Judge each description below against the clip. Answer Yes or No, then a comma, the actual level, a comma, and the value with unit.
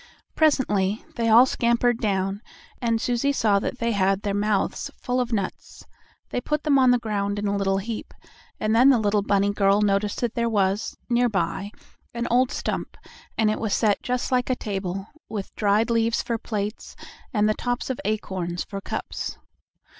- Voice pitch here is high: Yes, high, 215 Hz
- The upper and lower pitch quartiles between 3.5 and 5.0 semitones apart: No, average, 3.1 semitones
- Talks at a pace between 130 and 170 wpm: No, average, 180 wpm